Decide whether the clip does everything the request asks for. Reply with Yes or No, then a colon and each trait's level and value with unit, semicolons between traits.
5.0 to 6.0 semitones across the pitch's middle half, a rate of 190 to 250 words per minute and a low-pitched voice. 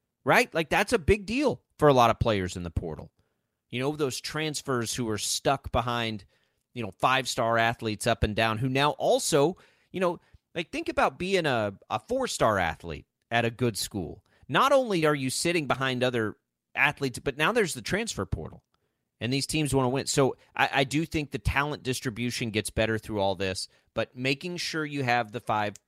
Yes: wide, 5.4 semitones; fast, 205 wpm; low, 130 Hz